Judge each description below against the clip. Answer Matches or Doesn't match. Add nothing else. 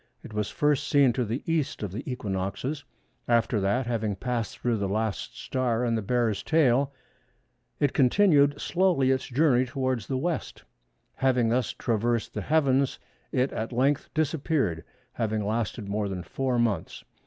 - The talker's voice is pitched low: Matches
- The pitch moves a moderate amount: Matches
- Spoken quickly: Doesn't match